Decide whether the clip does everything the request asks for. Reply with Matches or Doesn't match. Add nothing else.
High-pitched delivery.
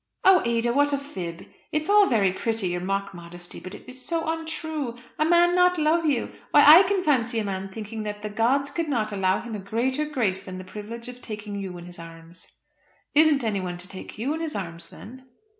Matches